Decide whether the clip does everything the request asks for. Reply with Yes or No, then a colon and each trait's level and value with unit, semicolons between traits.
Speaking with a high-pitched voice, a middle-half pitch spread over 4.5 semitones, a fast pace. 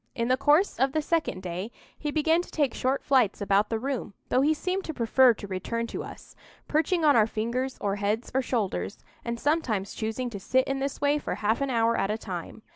Yes: high, 245 Hz; average, 4.9 semitones; fast, 225 wpm